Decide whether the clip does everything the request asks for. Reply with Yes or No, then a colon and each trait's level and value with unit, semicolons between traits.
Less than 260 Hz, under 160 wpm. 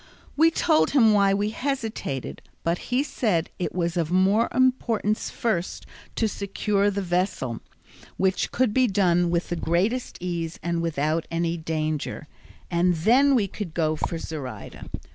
Yes: medium, 185 Hz; average, 150 wpm